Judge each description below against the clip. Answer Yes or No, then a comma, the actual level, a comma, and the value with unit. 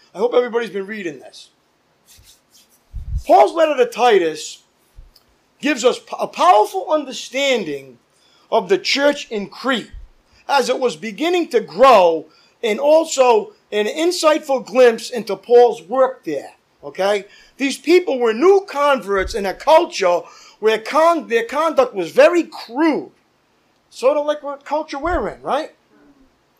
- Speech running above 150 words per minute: No, slow, 135 wpm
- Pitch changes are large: Yes, wide, 6.4 semitones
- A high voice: Yes, very high, 270 Hz